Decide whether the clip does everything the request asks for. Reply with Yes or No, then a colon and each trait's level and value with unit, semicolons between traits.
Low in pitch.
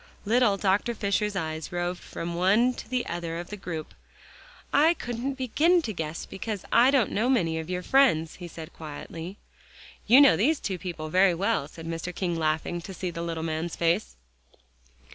No: medium, 180 Hz